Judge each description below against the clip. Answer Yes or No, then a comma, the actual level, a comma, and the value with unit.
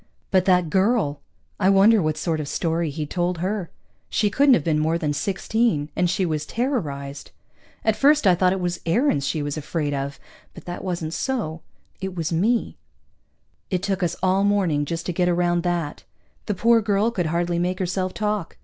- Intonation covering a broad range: No, average, 3.8 semitones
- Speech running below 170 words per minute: No, average, 190 wpm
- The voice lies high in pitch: No, medium, 180 Hz